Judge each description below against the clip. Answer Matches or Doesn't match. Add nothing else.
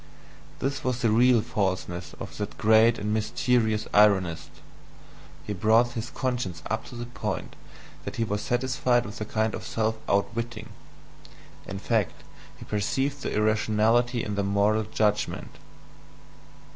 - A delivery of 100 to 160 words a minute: Matches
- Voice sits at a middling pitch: Doesn't match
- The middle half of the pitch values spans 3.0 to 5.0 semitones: Doesn't match